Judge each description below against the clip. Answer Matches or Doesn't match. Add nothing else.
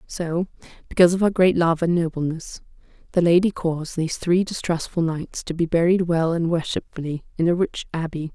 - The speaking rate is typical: Matches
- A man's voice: Doesn't match